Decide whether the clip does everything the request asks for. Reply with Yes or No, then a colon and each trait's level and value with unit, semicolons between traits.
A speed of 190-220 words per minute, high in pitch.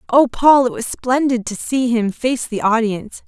Yes: average, 200 wpm; high, 240 Hz